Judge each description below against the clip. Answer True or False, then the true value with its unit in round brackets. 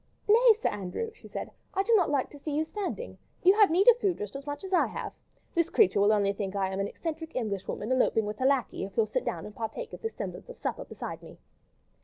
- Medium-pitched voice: False (285 Hz)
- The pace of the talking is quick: True (260 wpm)